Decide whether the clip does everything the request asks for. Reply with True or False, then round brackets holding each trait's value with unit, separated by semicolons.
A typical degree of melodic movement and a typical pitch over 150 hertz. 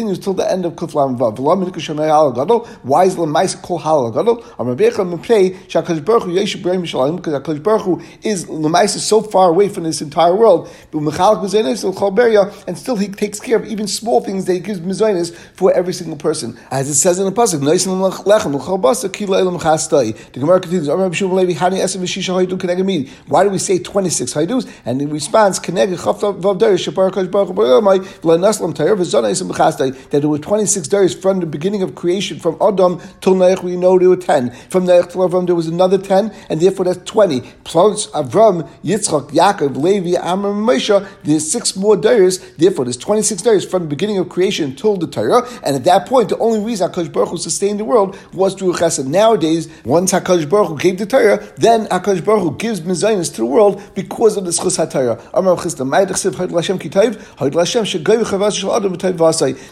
True (3.2 semitones; 185 Hz)